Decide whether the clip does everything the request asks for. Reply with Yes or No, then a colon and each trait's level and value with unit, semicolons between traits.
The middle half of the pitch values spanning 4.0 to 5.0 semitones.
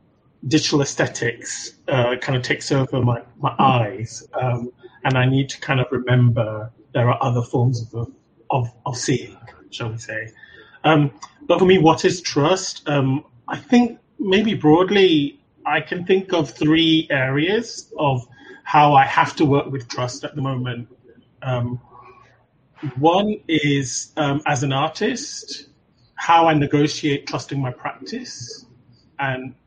Yes: average, 4.3 semitones